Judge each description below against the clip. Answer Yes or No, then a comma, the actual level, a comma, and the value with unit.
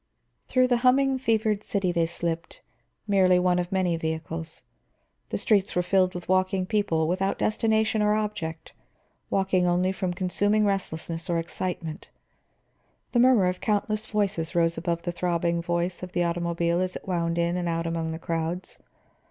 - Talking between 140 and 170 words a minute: Yes, average, 160 wpm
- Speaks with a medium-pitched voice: Yes, medium, 180 Hz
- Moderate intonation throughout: Yes, average, 3.1 semitones